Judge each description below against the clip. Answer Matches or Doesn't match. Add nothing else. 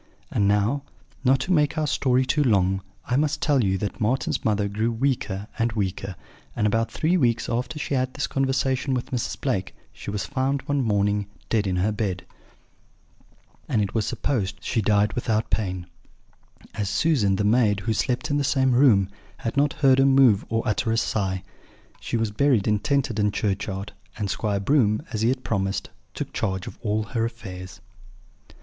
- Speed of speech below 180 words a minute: Doesn't match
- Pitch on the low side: Matches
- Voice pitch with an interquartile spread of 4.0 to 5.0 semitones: Matches